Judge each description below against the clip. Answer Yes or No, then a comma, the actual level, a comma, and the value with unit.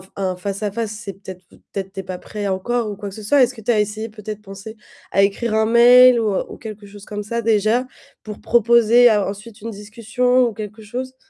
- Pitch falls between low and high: No, high, 215 Hz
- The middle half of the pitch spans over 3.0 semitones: No, average, 2.7 semitones